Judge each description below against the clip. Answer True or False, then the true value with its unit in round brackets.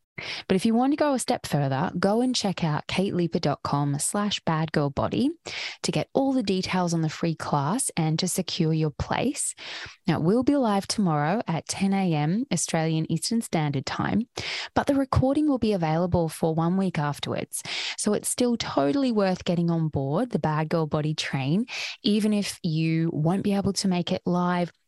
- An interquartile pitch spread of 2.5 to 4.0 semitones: False (4.8 semitones)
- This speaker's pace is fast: False (180 wpm)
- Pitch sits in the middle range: True (180 Hz)